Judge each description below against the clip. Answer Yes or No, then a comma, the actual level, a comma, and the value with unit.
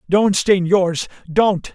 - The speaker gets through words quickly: No, slow, 105 wpm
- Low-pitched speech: No, medium, 185 Hz